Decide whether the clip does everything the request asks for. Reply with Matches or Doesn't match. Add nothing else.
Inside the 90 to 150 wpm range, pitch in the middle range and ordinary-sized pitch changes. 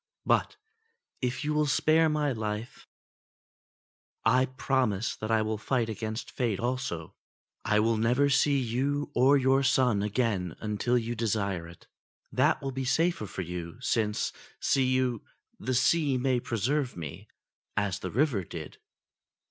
Doesn't match